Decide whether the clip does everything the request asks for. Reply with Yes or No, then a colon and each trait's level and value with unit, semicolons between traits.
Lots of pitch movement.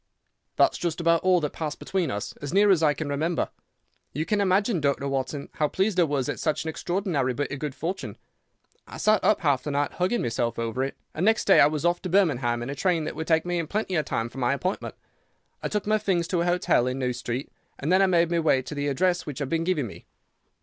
No: average, 4.6 semitones